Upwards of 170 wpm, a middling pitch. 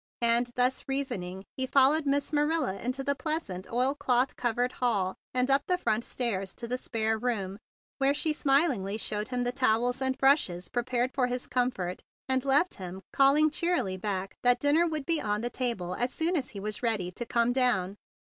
No: average, 190 wpm; high, 245 Hz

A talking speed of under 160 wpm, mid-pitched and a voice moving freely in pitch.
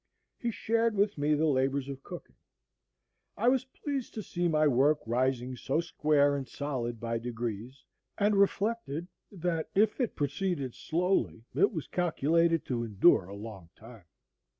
Yes: average, 150 wpm; medium, 150 Hz; wide, 7.0 semitones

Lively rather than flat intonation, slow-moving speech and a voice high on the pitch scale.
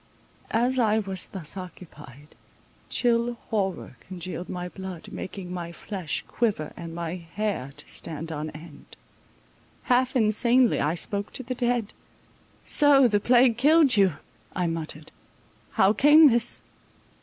Yes: wide, 6.0 semitones; slow, 130 wpm; high, 195 Hz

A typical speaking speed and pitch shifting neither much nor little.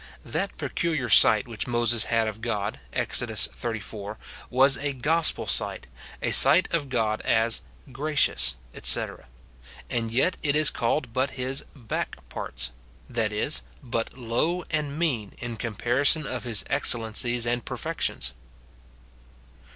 No: slow, 130 wpm; average, 3.9 semitones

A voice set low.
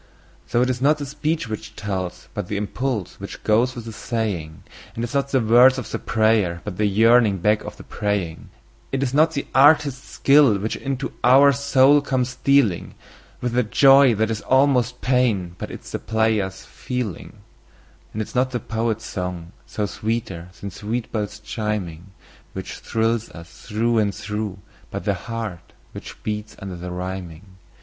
Yes: low, 110 Hz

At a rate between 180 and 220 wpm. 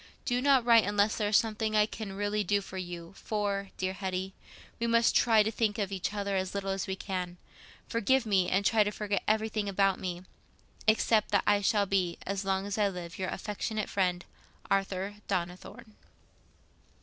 Yes: average, 185 wpm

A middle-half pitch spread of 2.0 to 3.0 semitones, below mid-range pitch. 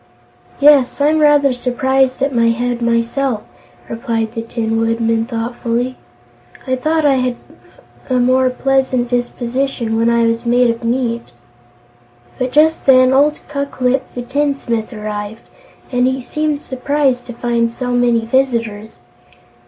No: narrow, 2.5 semitones; high, 245 Hz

